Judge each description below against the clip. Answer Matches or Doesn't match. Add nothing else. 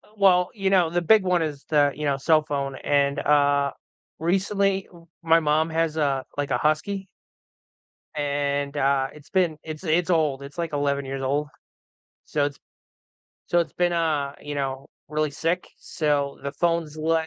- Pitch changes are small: Doesn't match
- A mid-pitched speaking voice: Matches